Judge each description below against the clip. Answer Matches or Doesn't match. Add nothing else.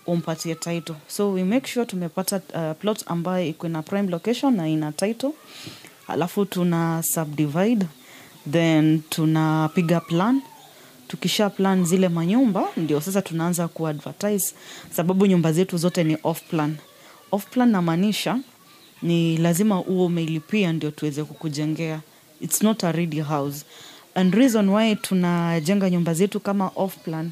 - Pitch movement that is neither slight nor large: Matches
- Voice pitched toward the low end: Doesn't match